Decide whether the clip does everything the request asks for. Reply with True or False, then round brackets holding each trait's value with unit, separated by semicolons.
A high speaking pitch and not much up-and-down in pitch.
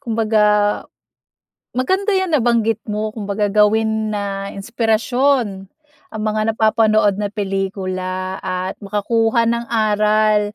True (215 Hz; 2.0 semitones)